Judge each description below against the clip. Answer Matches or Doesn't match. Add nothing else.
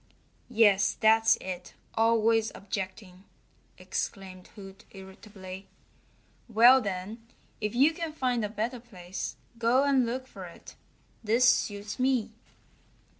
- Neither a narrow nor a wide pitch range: Matches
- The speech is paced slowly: Matches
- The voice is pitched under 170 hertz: Doesn't match